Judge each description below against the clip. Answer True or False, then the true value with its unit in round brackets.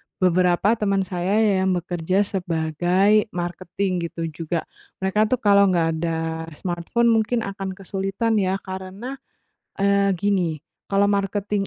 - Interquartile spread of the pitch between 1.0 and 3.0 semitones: True (2.5 semitones)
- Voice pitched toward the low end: False (190 Hz)